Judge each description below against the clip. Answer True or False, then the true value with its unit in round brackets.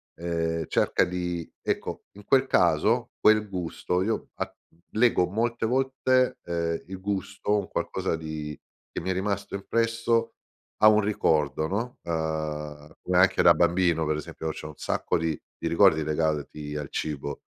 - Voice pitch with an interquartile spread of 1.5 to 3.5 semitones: False (5.3 semitones)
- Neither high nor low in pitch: False (90 Hz)